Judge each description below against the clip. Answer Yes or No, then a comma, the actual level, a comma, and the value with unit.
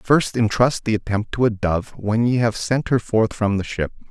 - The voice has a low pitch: Yes, low, 110 Hz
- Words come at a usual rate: No, fast, 235 wpm